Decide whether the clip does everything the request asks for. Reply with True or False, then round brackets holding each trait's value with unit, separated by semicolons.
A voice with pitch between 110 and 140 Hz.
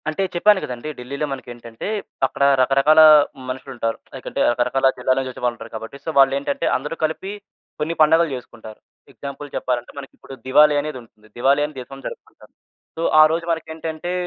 True (135 Hz)